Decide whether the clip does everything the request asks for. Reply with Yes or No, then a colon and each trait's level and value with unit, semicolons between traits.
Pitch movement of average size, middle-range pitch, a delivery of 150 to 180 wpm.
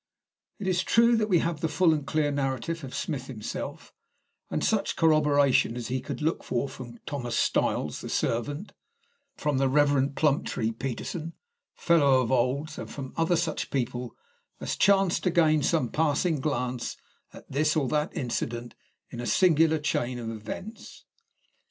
Yes: average, 4.2 semitones; medium, 145 Hz; average, 160 wpm